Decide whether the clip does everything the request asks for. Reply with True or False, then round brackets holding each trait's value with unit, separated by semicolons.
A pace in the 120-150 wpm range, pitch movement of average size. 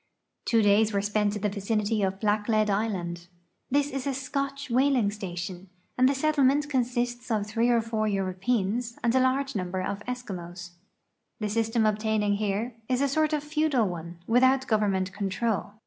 False (170 wpm; 4.1 semitones)